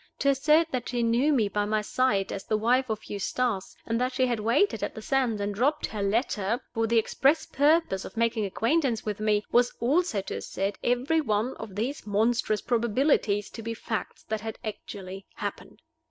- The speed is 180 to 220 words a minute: Yes, average, 190 wpm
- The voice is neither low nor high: No, high, 230 Hz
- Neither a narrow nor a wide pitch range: Yes, average, 3.7 semitones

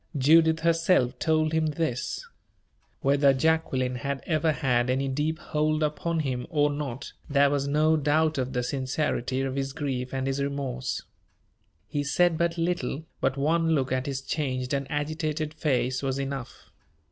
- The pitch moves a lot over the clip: No, average, 2.9 semitones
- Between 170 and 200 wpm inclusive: No, average, 160 wpm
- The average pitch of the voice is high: No, medium, 140 Hz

